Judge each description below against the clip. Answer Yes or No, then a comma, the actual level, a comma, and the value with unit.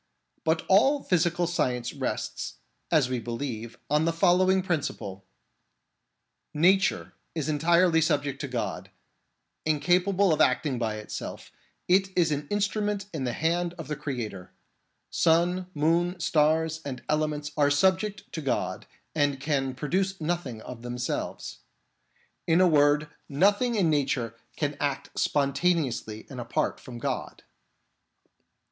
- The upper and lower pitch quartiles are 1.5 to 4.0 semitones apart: No, average, 4.5 semitones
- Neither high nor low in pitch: Yes, medium, 155 Hz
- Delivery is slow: Yes, slow, 130 wpm